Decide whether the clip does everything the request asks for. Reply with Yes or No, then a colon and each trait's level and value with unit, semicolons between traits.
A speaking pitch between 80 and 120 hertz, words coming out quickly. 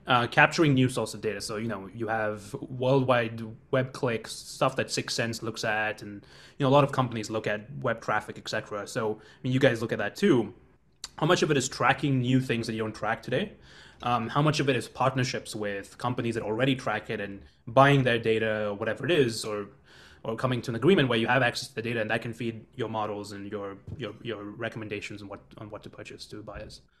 Yes: low, 115 Hz; fast, 240 wpm